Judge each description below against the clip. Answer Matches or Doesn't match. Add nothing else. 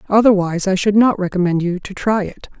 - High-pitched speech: Matches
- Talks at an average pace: Doesn't match